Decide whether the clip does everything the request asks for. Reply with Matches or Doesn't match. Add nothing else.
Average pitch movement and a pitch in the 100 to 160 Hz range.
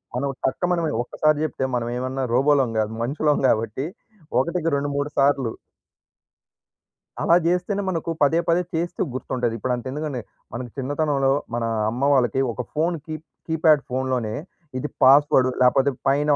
Matches